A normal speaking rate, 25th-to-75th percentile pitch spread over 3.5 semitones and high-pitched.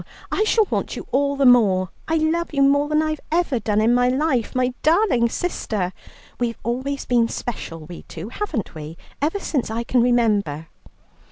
Yes: average, 180 wpm; wide, 5.6 semitones; high, 245 Hz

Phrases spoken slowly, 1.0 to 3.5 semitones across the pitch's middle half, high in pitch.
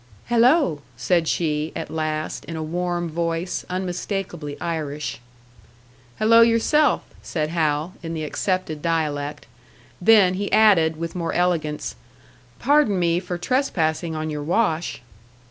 No: slow, 125 wpm; average, 3.1 semitones; medium, 170 Hz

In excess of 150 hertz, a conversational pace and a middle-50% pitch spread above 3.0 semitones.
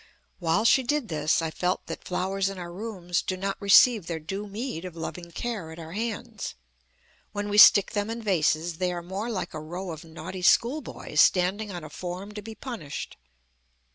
Yes: medium, 185 Hz; average, 195 wpm; average, 3.6 semitones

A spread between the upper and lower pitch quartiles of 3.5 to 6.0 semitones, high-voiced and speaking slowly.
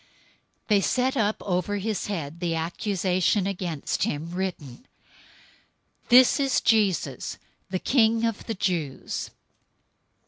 Yes: average, 4.2 semitones; high, 195 Hz; slow, 115 wpm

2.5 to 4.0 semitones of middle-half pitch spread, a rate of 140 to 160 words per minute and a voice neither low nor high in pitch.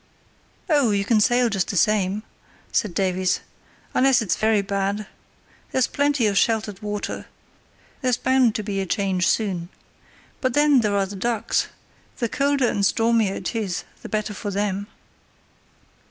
No: average, 3.3 semitones; average, 155 wpm; high, 210 Hz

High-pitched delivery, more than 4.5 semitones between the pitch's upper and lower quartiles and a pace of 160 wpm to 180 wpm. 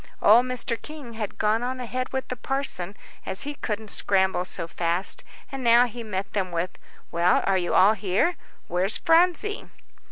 Yes: high, 220 Hz; average, 5.1 semitones; average, 170 wpm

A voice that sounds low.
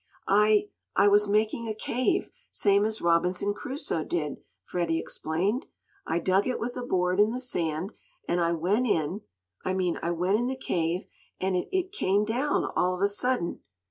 No: high, 200 Hz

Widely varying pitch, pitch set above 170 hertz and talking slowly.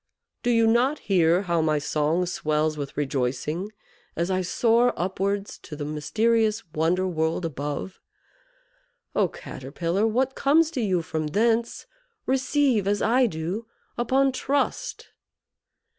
Yes: wide, 6.7 semitones; high, 190 Hz; slow, 130 wpm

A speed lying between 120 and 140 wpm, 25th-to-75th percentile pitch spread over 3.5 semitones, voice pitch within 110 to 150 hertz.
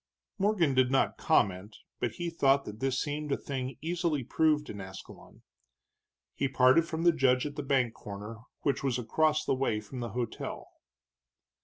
No: average, 170 wpm; average, 4.1 semitones; low, 135 Hz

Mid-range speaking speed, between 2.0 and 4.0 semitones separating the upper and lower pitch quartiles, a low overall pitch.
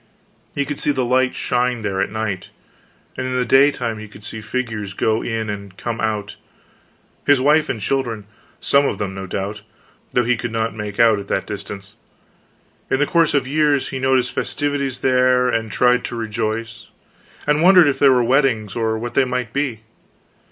Yes: average, 185 wpm; average, 3.5 semitones; low, 120 Hz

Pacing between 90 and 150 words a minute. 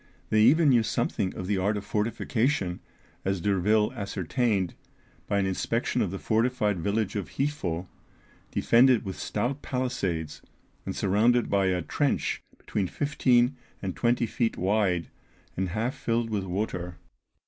Yes: average, 140 wpm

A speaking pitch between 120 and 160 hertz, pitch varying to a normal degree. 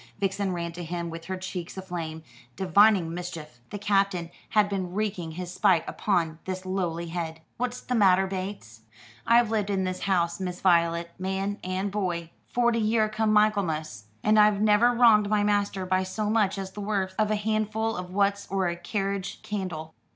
No: high, 190 Hz; average, 3.1 semitones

